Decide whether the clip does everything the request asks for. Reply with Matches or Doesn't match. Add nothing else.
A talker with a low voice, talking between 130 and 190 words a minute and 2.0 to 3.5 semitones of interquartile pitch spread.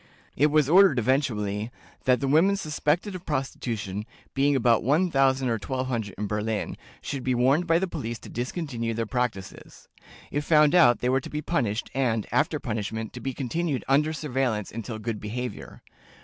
Doesn't match